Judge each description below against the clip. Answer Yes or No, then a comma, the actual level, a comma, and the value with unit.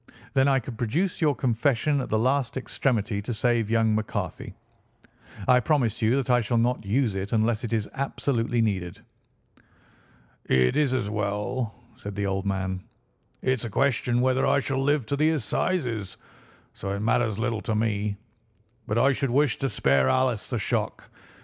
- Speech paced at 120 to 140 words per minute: No, average, 170 wpm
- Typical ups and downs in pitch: Yes, average, 3.9 semitones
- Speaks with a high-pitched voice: No, low, 120 Hz